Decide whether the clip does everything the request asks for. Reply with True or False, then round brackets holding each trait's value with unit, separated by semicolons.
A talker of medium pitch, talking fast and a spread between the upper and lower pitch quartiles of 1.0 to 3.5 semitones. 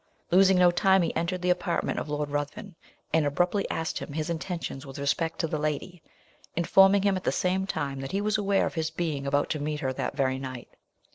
False (165 Hz; 220 wpm; 4.2 semitones)